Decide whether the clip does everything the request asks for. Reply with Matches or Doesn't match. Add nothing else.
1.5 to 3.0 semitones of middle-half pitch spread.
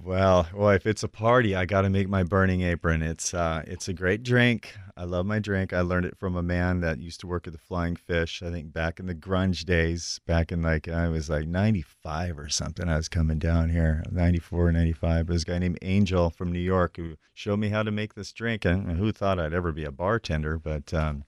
Matches